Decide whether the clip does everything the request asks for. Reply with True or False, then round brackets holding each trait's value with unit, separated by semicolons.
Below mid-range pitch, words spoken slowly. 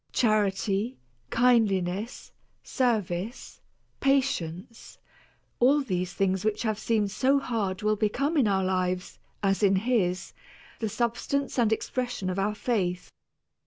False (215 Hz; 120 wpm)